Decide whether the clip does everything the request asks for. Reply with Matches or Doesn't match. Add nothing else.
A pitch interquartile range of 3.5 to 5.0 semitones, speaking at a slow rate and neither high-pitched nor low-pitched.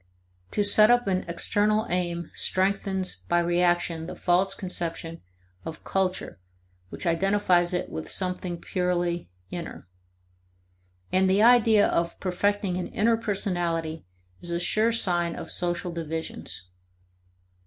Doesn't match